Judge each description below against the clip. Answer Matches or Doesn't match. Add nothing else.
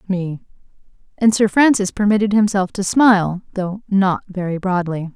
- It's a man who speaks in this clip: Doesn't match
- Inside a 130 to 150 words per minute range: Matches